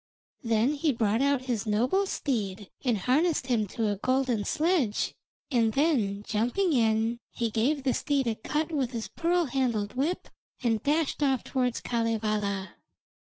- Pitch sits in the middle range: No, high, 245 Hz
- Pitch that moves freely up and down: No, average, 4.4 semitones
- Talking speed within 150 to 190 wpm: Yes, average, 155 wpm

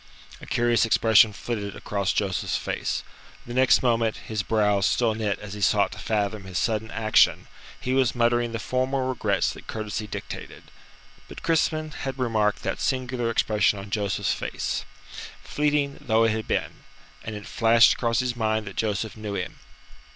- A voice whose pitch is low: Yes, low, 110 Hz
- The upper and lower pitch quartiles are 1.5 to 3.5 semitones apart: Yes, narrow, 2.6 semitones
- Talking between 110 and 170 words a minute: Yes, average, 165 wpm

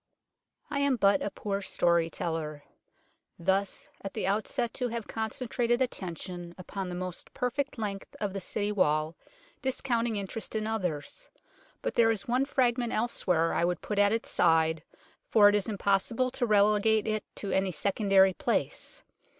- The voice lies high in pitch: Yes, high, 205 Hz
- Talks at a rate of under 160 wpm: No, average, 165 wpm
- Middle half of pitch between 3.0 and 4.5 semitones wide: Yes, average, 4.1 semitones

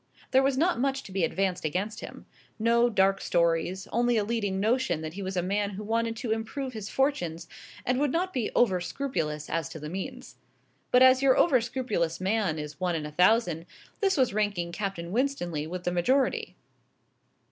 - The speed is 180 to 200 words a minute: Yes, average, 190 wpm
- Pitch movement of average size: No, wide, 6.2 semitones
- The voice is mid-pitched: No, high, 205 Hz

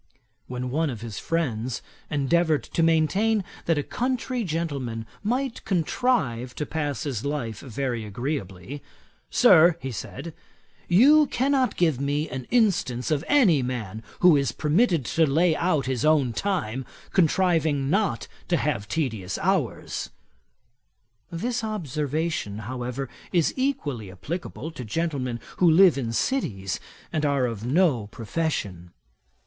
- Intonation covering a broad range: Yes, wide, 6.2 semitones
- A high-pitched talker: No, medium, 150 Hz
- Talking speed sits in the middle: No, slow, 130 wpm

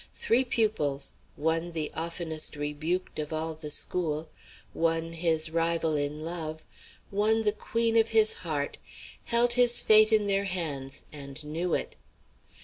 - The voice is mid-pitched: Yes, medium, 165 Hz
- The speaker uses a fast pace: No, average, 140 wpm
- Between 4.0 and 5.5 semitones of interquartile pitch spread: Yes, average, 5.2 semitones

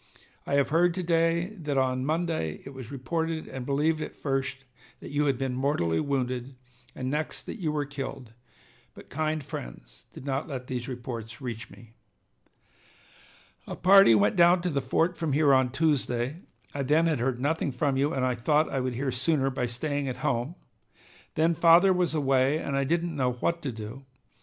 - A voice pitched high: No, medium, 140 Hz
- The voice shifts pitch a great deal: No, average, 3.7 semitones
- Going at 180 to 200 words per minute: Yes, average, 190 wpm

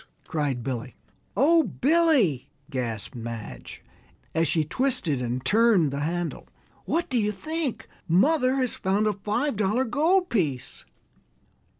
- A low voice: No, high, 200 Hz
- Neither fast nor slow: No, slow, 125 wpm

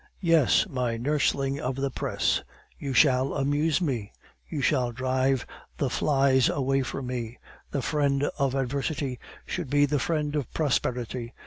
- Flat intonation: Yes, narrow, 2.2 semitones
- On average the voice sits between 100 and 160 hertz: Yes, low, 135 Hz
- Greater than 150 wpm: No, average, 145 wpm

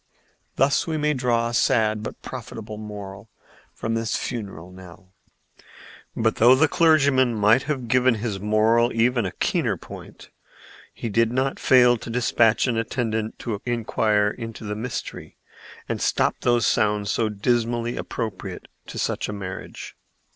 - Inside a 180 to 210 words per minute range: No, average, 145 wpm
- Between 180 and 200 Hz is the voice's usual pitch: No, low, 115 Hz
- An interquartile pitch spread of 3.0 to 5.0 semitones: No, narrow, 2.5 semitones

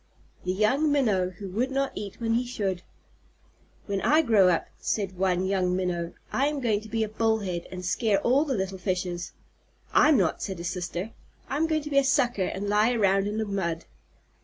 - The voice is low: No, high, 205 Hz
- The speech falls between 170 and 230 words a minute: Yes, average, 200 wpm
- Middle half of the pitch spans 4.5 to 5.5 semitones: Yes, average, 4.8 semitones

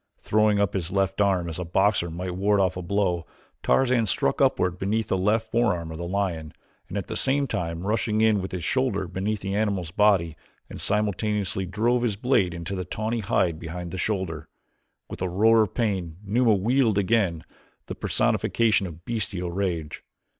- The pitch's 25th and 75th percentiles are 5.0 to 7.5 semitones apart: No, average, 3.4 semitones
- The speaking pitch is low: Yes, low, 100 Hz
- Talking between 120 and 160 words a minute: No, average, 180 wpm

